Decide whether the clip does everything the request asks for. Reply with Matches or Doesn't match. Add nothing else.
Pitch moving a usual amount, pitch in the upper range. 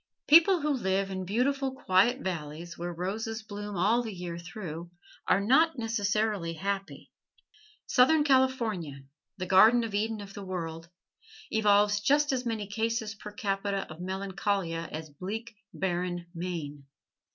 Matches